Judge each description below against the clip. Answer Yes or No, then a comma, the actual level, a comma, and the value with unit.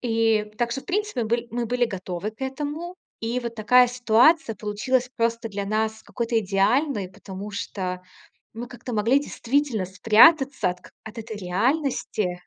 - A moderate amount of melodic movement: Yes, average, 3.3 semitones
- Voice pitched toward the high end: Yes, high, 230 Hz